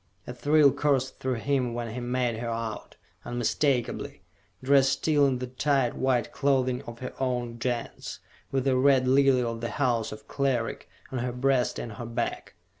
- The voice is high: No, low, 125 Hz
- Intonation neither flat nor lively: No, narrow, 2.3 semitones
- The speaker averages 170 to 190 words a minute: Yes, average, 180 wpm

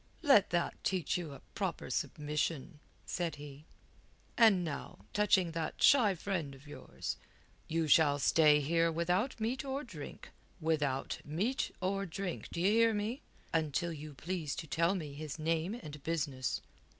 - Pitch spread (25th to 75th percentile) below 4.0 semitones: No, average, 4.7 semitones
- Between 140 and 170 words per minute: Yes, average, 150 wpm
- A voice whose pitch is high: No, medium, 165 Hz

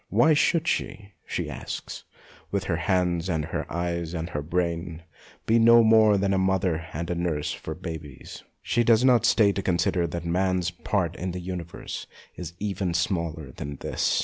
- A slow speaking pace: No, average, 175 wpm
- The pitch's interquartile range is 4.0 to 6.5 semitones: No, average, 2.8 semitones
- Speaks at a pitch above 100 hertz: No, very low, 90 Hz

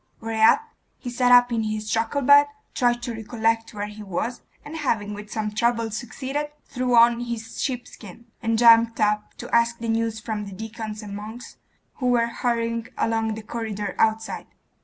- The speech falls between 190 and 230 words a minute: No, average, 175 wpm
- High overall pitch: Yes, high, 230 Hz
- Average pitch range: No, narrow, 1.8 semitones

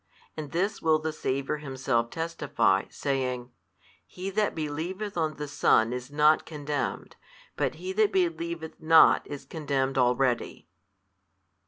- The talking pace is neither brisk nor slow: No, slow, 130 wpm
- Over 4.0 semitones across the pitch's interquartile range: No, average, 3.7 semitones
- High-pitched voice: No, medium, 150 Hz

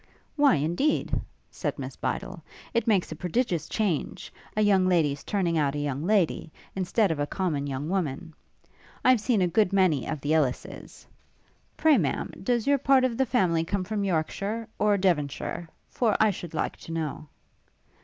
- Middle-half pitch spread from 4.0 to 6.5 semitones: Yes, wide, 5.4 semitones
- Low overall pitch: No, medium, 185 Hz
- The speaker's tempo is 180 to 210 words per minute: No, average, 170 wpm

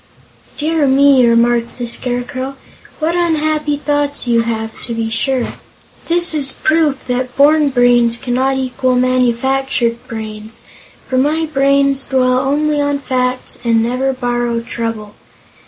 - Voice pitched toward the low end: No, very high, 255 Hz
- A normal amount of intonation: Yes, average, 3.0 semitones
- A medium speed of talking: No, slow, 130 wpm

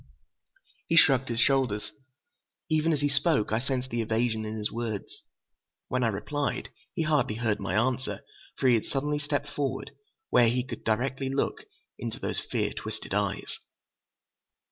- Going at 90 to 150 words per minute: No, average, 160 wpm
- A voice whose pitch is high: No, low, 130 Hz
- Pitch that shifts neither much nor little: Yes, average, 4.0 semitones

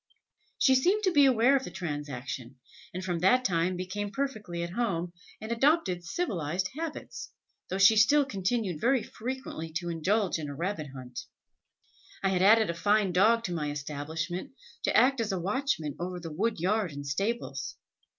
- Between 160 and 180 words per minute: Yes, average, 170 wpm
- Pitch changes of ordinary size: No, wide, 5.7 semitones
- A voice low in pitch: No, high, 190 Hz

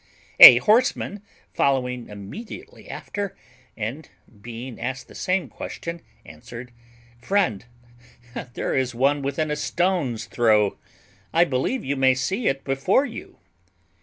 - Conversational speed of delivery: No, slow, 120 wpm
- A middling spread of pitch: No, wide, 7.0 semitones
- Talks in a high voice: No, low, 135 Hz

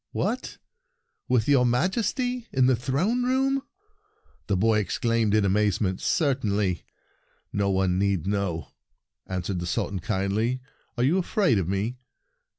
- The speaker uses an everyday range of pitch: No, wide, 6.2 semitones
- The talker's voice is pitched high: No, low, 110 Hz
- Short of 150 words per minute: Yes, slow, 135 wpm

